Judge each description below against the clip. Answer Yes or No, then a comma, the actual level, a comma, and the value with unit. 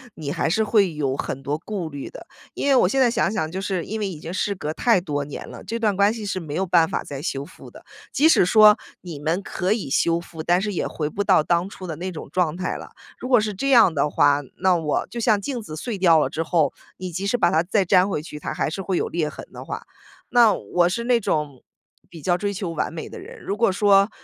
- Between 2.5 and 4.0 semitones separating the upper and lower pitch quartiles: No, average, 4.6 semitones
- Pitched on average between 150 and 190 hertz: Yes, medium, 185 Hz